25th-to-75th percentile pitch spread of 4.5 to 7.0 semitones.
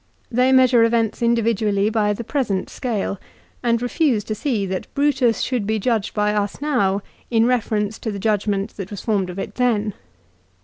No: average, 3.1 semitones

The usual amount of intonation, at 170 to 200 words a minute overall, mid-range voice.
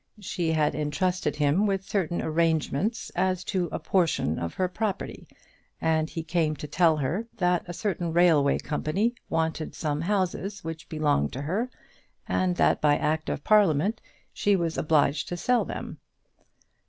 No: average, 3.5 semitones; average, 155 wpm; medium, 165 Hz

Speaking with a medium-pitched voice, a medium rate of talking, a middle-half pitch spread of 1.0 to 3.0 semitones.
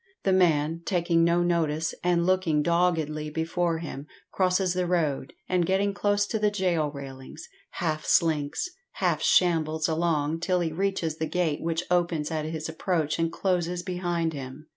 Yes: medium, 170 Hz; average, 160 wpm; narrow, 2.4 semitones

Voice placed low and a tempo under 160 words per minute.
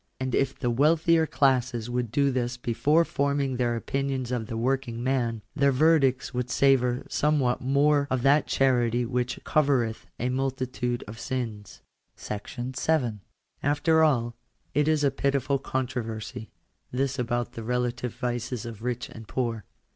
Yes: low, 125 Hz; average, 150 wpm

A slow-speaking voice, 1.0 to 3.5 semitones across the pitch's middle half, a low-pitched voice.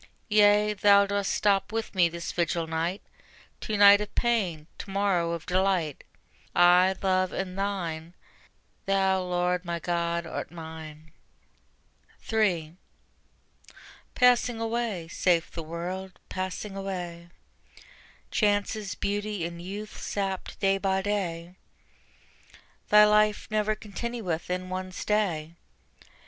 No: slow, 115 wpm; average, 3.1 semitones; high, 190 Hz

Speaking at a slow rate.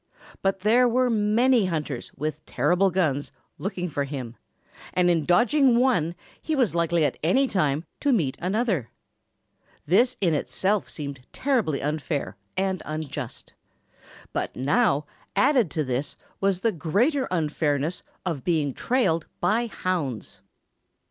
Yes: slow, 130 wpm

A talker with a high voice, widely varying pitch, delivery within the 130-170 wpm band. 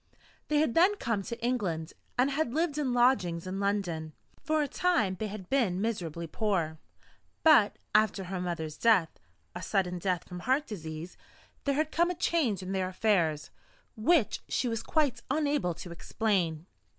Yes: high, 210 Hz; wide, 7.4 semitones; average, 165 wpm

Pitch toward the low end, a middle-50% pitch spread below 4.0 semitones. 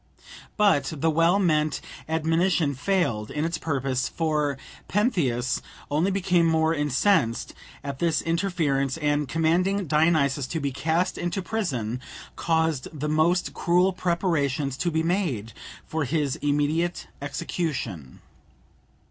No: medium, 160 Hz; average, 3.6 semitones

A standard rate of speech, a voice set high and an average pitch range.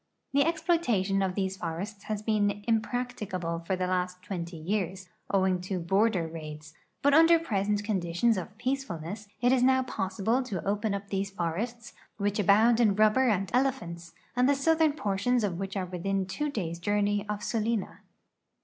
Yes: average, 165 wpm; high, 205 Hz; average, 4.4 semitones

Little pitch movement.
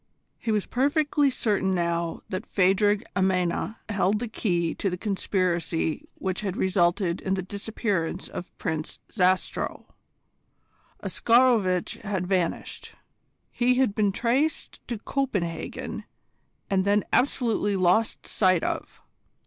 No: average, 3.5 semitones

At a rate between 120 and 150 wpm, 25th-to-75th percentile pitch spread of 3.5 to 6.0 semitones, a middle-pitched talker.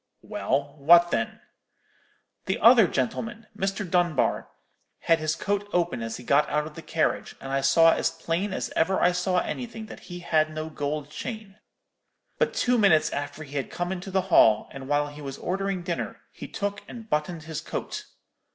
No: average, 185 wpm; average, 4.8 semitones; medium, 170 Hz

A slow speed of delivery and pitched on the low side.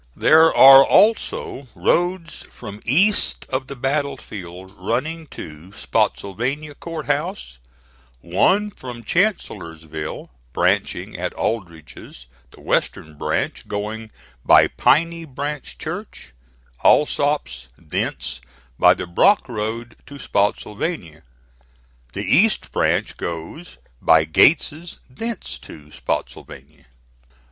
Yes: slow, 100 wpm; low, 125 Hz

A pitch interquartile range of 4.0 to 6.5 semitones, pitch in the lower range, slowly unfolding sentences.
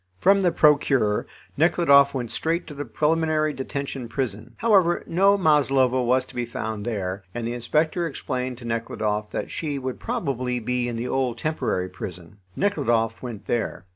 No: average, 5.0 semitones; low, 130 Hz; average, 165 wpm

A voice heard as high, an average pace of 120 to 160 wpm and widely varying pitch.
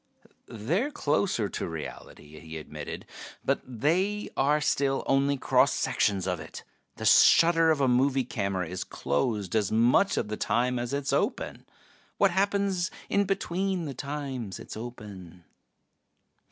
No: low, 130 Hz; average, 145 wpm; wide, 8.1 semitones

